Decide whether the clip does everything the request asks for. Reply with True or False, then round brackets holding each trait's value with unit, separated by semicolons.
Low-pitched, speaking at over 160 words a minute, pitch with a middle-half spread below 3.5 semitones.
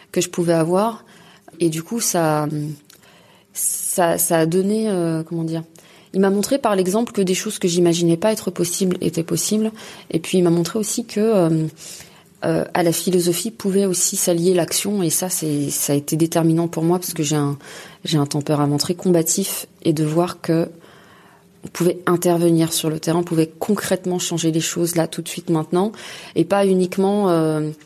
False (175 Hz; 190 wpm; 2.8 semitones)